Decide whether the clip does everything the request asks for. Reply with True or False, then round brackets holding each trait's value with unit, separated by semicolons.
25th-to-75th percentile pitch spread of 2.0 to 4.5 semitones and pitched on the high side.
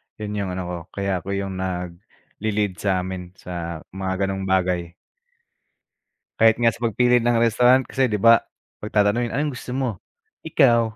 False (4.0 semitones; 100 Hz)